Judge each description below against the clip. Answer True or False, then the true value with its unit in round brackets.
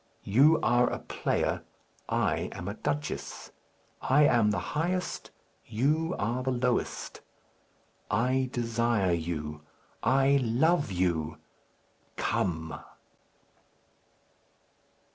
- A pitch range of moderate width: False (6.4 semitones)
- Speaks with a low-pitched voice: True (120 Hz)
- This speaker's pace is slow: True (90 wpm)